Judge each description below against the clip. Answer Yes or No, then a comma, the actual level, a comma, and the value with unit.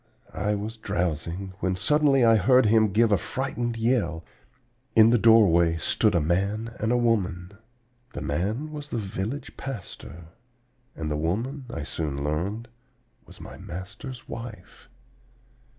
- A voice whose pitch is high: No, low, 105 Hz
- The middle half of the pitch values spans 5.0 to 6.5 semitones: Yes, average, 5.3 semitones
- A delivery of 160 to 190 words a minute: No, average, 140 wpm